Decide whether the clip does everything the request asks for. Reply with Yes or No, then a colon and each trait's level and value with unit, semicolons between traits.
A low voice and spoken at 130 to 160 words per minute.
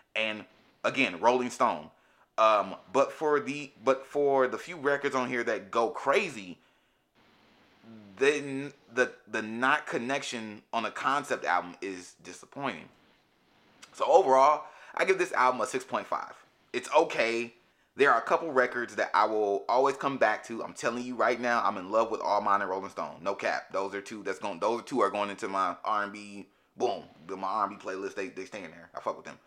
No: low, 125 Hz; average, 185 wpm